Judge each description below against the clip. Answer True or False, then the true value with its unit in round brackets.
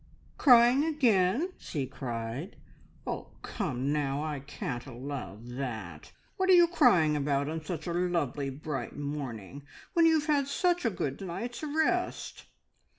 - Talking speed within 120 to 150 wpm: True (145 wpm)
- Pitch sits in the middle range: True (155 Hz)